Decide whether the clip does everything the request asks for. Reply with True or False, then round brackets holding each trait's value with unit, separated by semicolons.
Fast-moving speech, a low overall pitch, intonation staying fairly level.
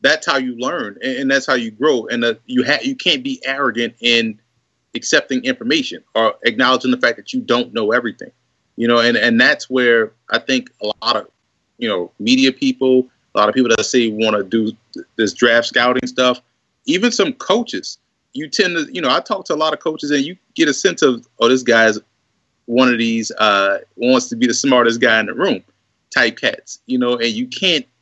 False (220 wpm; 125 Hz; 3.9 semitones)